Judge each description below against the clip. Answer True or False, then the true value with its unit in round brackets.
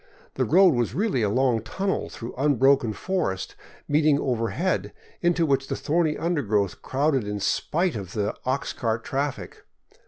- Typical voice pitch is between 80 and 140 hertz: True (135 Hz)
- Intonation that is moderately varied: False (6.0 semitones)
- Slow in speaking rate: False (155 wpm)